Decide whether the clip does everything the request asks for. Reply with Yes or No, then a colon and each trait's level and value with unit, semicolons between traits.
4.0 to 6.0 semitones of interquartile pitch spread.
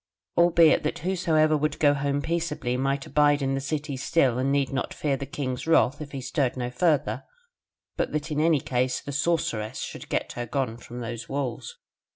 No: average, 3.2 semitones